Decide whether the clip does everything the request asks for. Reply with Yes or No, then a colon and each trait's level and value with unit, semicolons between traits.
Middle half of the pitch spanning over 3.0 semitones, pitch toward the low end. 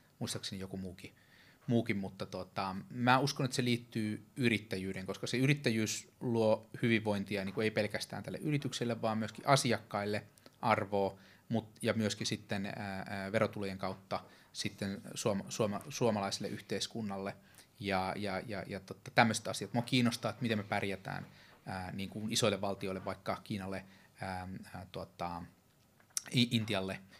Yes: average, 3.4 semitones; low, 105 Hz